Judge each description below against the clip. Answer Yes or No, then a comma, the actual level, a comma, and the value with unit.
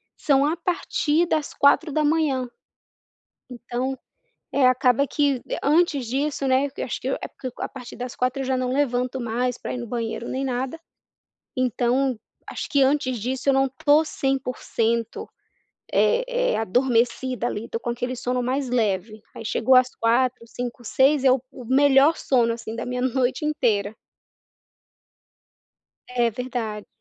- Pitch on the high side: Yes, very high, 255 Hz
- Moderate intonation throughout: No, narrow, 2.3 semitones